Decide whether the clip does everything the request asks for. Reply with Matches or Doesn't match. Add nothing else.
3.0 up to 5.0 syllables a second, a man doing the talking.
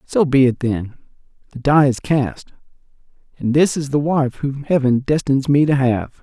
Matches